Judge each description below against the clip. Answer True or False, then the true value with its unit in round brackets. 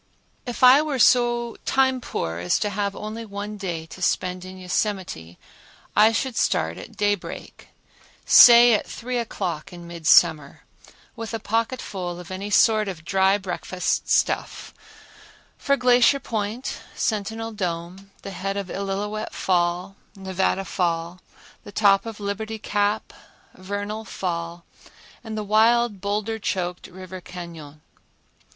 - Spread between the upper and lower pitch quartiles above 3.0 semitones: True (3.5 semitones)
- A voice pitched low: False (200 Hz)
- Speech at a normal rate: False (130 wpm)